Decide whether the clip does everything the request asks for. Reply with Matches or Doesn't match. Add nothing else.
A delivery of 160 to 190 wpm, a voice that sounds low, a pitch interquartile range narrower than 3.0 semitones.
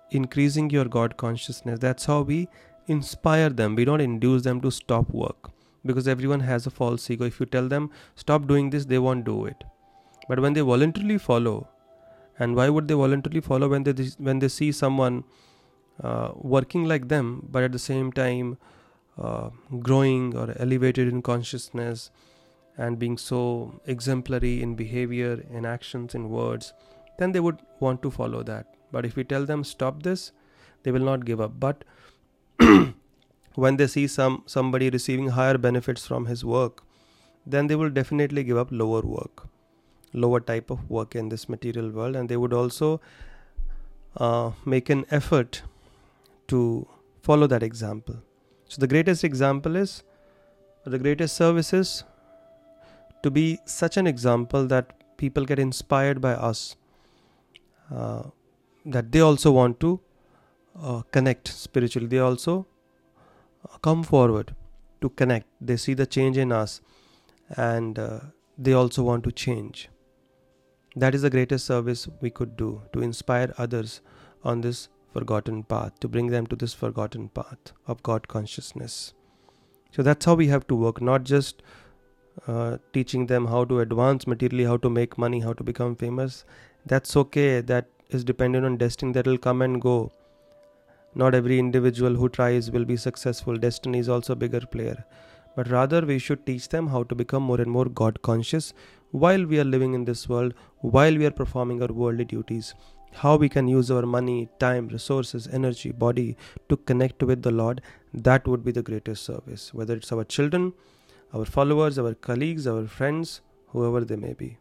Matches